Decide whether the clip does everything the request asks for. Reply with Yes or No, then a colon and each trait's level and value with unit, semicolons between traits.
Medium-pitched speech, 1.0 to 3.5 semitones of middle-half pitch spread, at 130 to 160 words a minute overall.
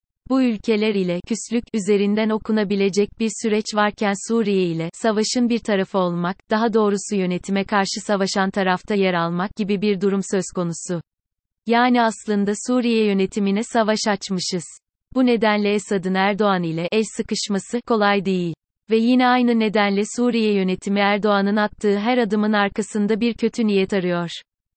No: high, 205 Hz; narrow, 2.4 semitones; fast, 140 wpm